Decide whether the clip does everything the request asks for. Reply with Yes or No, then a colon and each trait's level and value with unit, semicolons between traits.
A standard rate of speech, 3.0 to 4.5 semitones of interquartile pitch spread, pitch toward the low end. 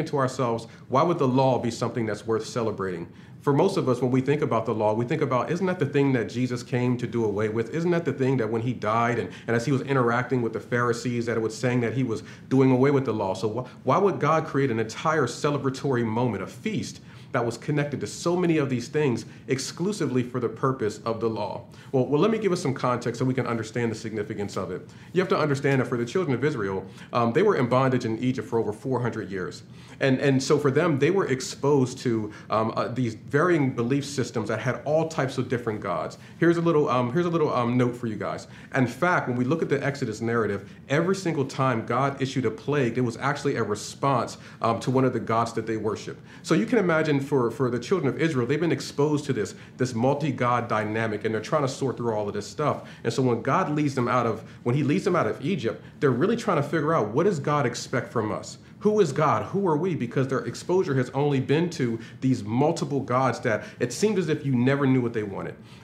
No: fast, 250 wpm; average, 3.9 semitones; low, 130 Hz